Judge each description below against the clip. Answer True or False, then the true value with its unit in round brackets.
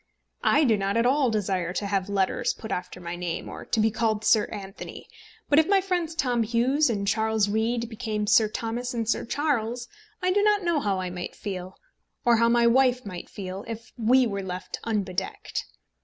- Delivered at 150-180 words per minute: False (200 wpm)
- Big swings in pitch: False (3.8 semitones)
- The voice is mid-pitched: False (220 Hz)